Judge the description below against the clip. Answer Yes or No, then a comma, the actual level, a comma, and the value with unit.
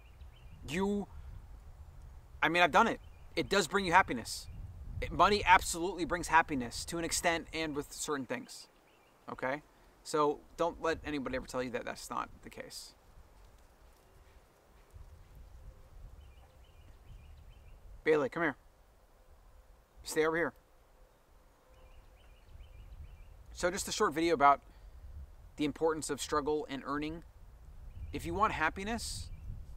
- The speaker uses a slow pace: Yes, slow, 115 wpm